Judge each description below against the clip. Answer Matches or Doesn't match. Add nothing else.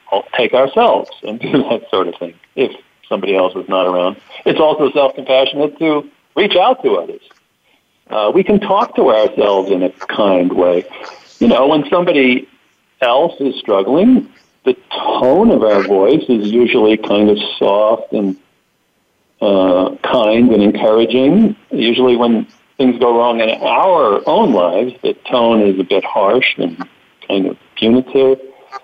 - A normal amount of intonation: Doesn't match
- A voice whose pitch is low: Matches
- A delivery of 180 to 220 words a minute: Doesn't match